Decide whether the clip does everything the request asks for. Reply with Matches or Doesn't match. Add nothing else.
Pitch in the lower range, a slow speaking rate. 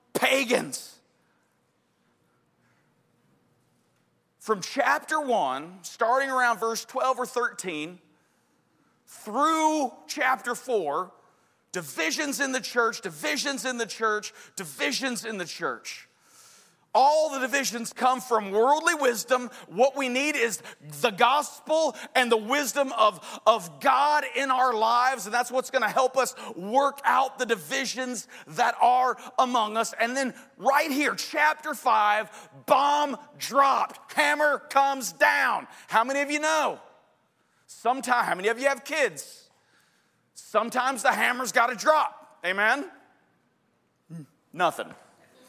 Doesn't match